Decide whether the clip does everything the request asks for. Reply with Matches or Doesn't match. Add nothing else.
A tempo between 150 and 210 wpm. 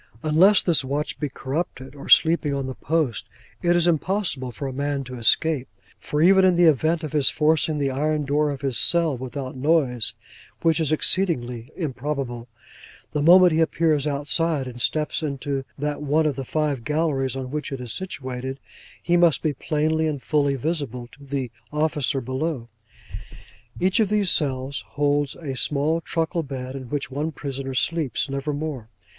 Matches